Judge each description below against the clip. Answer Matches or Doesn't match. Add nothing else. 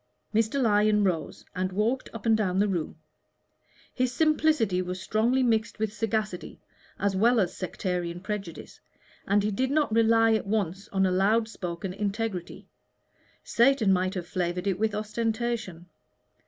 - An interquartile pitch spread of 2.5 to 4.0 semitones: Matches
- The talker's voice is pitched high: Matches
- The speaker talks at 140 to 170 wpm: Matches